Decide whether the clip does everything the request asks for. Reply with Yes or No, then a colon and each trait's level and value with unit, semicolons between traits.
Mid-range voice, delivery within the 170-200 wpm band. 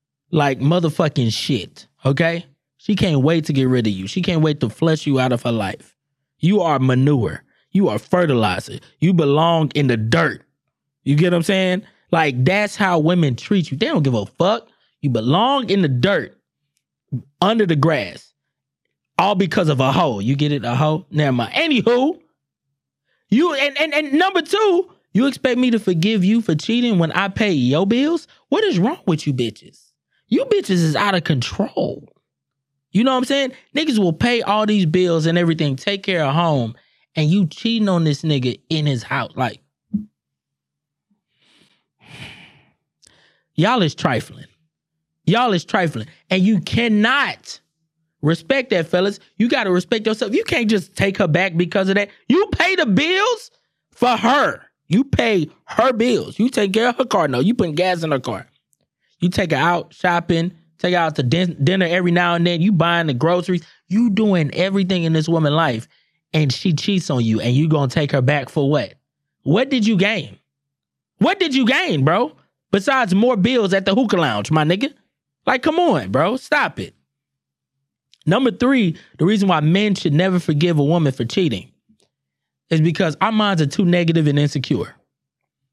Yes: medium, 170 Hz; average, 185 wpm